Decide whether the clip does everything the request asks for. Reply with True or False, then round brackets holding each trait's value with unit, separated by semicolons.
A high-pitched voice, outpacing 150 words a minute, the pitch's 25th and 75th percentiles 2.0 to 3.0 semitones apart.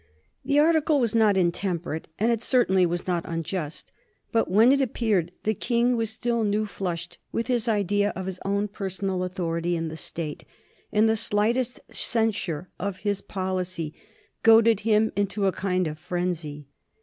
False (200 Hz; 160 wpm; 4.1 semitones)